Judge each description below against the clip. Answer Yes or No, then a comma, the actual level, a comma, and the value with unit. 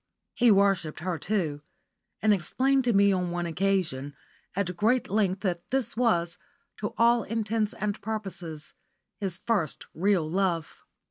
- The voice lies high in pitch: Yes, high, 195 Hz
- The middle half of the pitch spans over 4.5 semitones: No, average, 4.0 semitones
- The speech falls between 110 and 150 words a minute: Yes, average, 140 wpm